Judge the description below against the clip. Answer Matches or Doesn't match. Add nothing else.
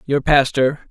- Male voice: Matches